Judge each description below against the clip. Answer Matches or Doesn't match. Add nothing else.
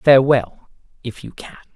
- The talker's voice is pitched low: Matches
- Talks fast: Doesn't match